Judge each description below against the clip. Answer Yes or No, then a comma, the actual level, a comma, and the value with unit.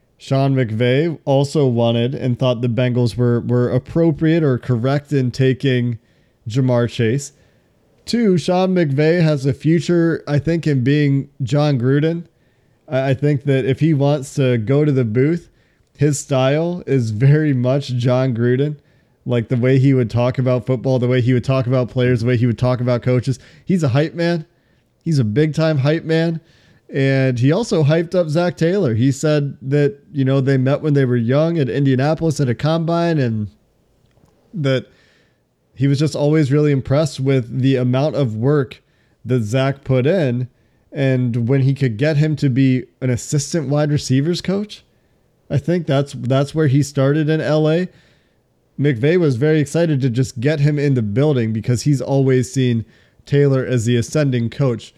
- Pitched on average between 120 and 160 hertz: Yes, low, 135 Hz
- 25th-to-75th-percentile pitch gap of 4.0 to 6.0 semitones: No, average, 3.2 semitones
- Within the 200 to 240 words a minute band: No, average, 175 wpm